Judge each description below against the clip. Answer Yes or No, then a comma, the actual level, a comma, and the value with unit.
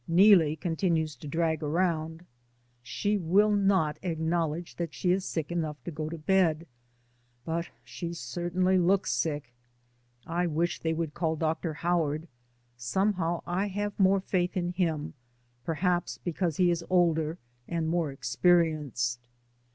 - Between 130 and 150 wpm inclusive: Yes, slow, 135 wpm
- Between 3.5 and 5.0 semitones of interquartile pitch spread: No, narrow, 2.4 semitones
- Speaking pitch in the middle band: Yes, medium, 170 Hz